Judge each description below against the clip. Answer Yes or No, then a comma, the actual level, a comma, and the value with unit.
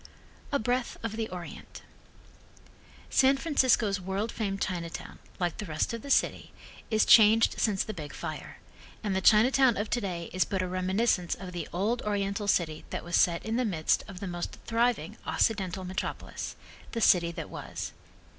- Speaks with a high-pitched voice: Yes, high, 200 Hz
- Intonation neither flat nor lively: Yes, average, 4.0 semitones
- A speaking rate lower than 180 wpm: Yes, average, 170 wpm